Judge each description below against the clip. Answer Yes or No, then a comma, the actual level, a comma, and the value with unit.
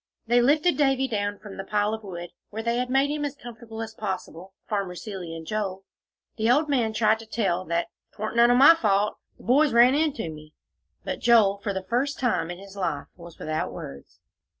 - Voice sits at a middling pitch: No, high, 220 Hz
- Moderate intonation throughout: Yes, average, 4.3 semitones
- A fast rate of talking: Yes, fast, 210 wpm